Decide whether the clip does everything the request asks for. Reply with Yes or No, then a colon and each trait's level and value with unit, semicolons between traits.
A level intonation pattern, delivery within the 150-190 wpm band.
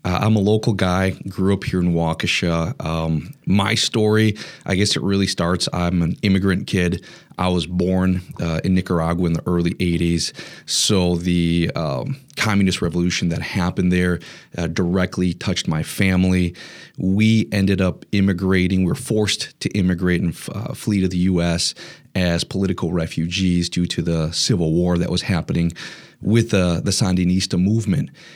Yes: narrow, 2.2 semitones; average, 155 wpm